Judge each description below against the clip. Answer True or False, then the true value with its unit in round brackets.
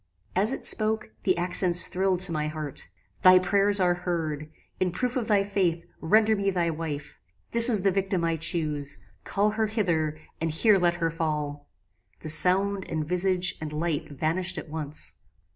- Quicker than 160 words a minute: True (175 wpm)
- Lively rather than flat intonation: False (3.9 semitones)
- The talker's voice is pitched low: False (175 Hz)